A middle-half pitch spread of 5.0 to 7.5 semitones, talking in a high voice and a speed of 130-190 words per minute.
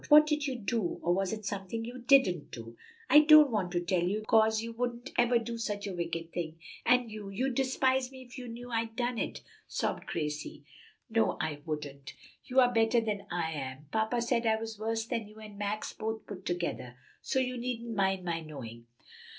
No: wide, 5.5 semitones; high, 220 Hz; fast, 205 wpm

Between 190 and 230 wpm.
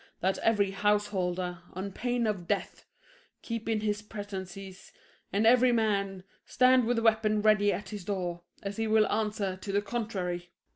No: average, 160 wpm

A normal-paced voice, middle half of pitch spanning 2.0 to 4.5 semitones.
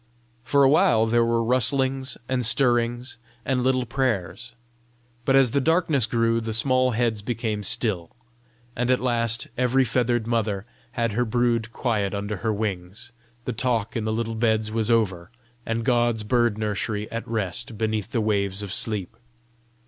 Yes: average, 160 wpm; narrow, 2.4 semitones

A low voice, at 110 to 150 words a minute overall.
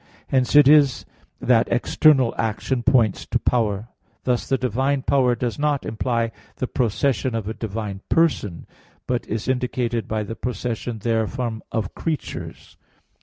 Yes: low, 120 Hz; average, 140 wpm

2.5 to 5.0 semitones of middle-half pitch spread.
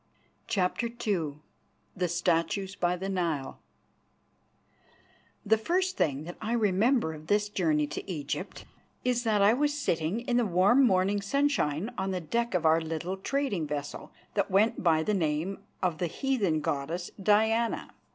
No: wide, 5.4 semitones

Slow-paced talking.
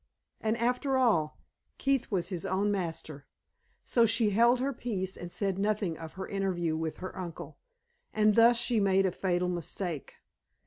No: average, 165 wpm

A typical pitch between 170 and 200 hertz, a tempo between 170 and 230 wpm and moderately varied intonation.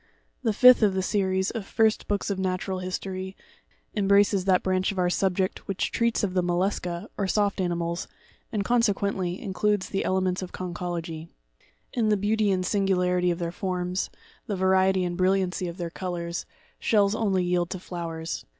No: high, 190 Hz; average, 175 wpm; narrow, 1.9 semitones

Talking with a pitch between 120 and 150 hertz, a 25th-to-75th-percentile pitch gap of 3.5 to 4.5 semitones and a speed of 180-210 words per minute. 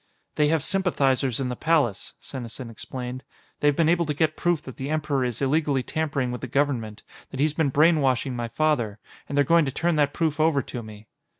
Yes: medium, 140 Hz; average, 3.8 semitones; fast, 205 wpm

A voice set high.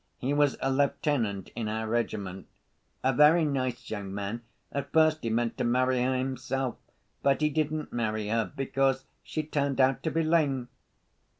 No: low, 130 Hz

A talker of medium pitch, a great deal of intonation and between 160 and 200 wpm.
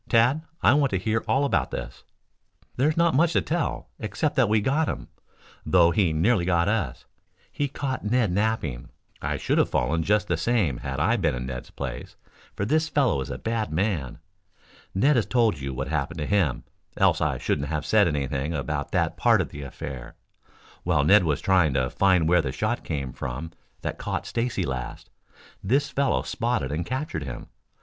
No: very low, 95 Hz; wide, 8.5 semitones; average, 190 wpm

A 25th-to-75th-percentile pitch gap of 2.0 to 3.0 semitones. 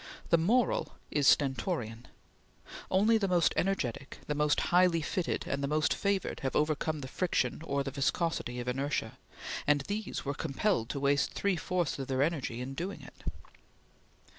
No: average, 4.8 semitones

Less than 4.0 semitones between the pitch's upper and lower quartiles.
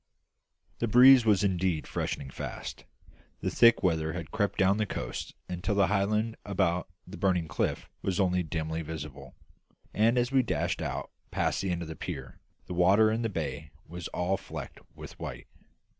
No: average, 4.4 semitones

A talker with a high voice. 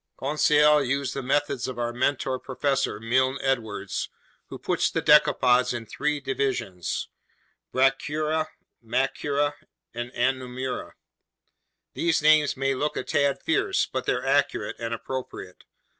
No: low, 135 Hz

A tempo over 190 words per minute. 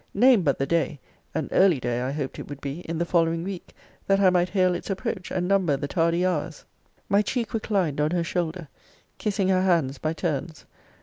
Yes: fast, 205 wpm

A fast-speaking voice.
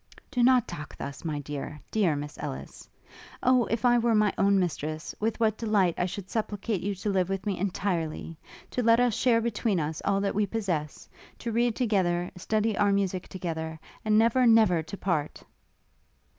No: average, 185 wpm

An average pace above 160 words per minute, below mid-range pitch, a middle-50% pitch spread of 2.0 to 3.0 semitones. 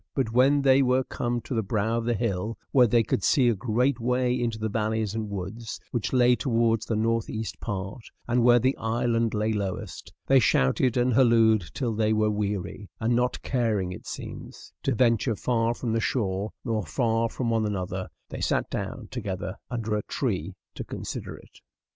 Yes: average, 190 wpm; low, 115 Hz; narrow, 2.4 semitones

